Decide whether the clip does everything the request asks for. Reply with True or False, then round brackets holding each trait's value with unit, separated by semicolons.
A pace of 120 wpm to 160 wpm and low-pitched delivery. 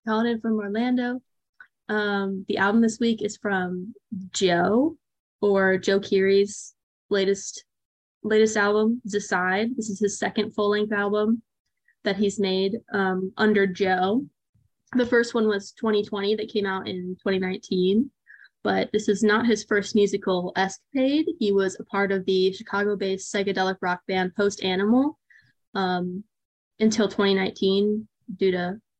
False (135 wpm; 205 Hz)